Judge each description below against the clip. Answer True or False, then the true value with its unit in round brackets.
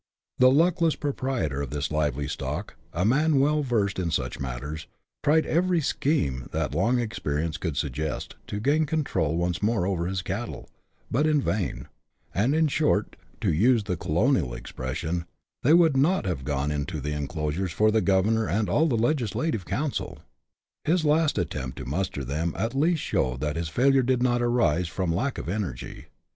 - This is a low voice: True (100 Hz)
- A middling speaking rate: True (180 wpm)